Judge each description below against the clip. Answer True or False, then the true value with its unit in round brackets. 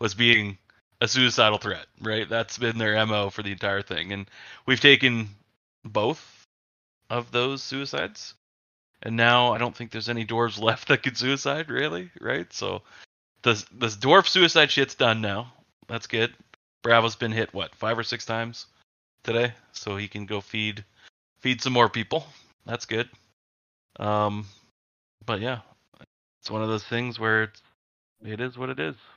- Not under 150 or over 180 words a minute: True (165 wpm)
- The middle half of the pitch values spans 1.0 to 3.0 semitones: True (2.7 semitones)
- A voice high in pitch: False (115 Hz)